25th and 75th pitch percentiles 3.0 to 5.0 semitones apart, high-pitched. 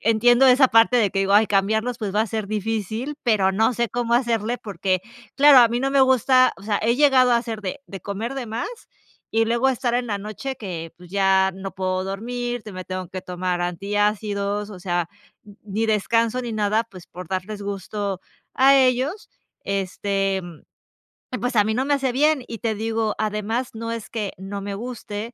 Yes: average, 3.6 semitones; high, 215 Hz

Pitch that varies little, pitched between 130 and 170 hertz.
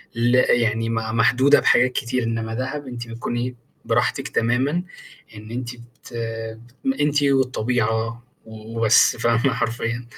No: narrow, 2.0 semitones; low, 120 Hz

